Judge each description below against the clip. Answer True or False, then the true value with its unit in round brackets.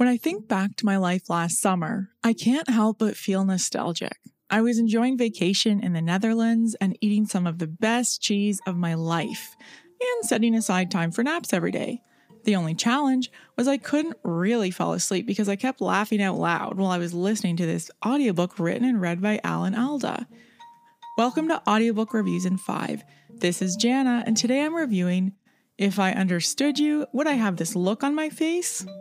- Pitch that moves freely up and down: False (4.8 semitones)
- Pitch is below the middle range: False (215 Hz)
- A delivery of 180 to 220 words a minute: True (190 wpm)